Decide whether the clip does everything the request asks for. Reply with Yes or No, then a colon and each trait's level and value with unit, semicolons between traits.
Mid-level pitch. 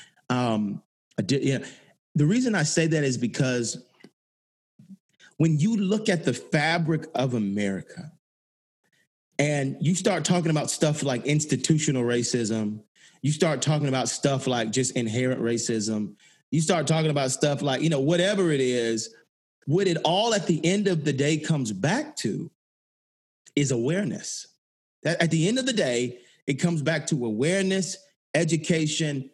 Yes: medium, 145 Hz